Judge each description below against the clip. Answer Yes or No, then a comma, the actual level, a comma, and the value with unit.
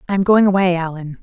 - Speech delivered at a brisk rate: Yes, fast, 245 wpm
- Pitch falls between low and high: Yes, medium, 180 Hz